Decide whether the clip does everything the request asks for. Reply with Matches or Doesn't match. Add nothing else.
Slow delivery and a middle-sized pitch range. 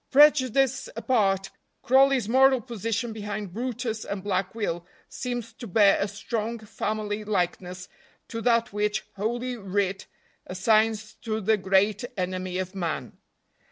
Matches